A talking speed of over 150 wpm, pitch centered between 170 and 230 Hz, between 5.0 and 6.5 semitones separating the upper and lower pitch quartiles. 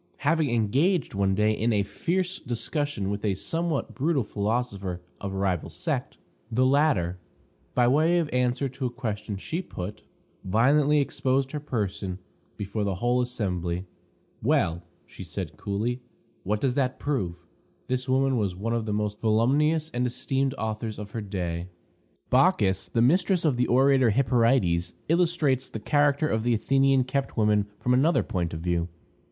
No: average, 160 wpm; low, 120 Hz; average, 5.3 semitones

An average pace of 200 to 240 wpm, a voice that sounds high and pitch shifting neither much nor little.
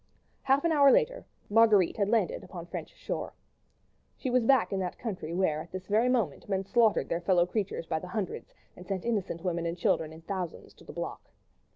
Yes: fast, 205 wpm; high, 195 Hz; average, 5.0 semitones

